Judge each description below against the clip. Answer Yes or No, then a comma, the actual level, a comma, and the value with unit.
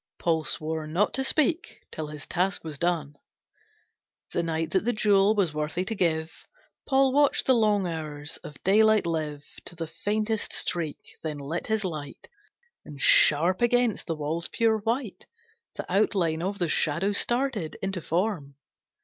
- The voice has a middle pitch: Yes, medium, 175 Hz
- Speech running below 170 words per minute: Yes, average, 160 wpm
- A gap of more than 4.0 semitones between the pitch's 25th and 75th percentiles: Yes, wide, 5.4 semitones